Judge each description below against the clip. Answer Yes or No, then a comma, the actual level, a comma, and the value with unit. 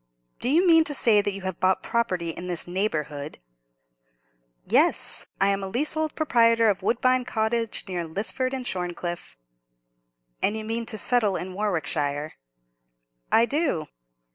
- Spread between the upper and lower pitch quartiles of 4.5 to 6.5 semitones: Yes, average, 5.2 semitones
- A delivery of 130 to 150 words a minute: Yes, average, 140 wpm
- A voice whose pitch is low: No, high, 210 Hz